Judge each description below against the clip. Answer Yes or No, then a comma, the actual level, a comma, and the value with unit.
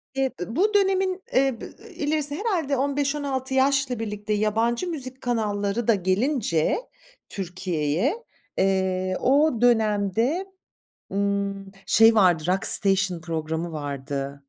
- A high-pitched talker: Yes, high, 220 Hz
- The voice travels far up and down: Yes, wide, 6.7 semitones